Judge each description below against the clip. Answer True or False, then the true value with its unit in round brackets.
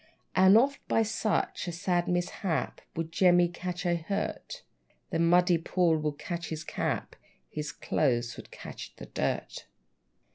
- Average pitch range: False (2.3 semitones)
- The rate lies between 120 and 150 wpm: True (145 wpm)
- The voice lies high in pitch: False (175 Hz)